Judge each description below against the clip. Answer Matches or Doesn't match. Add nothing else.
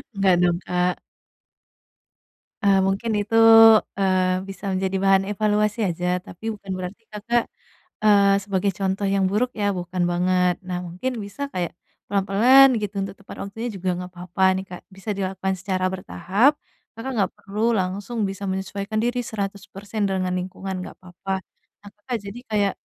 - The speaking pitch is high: Matches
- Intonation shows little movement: Matches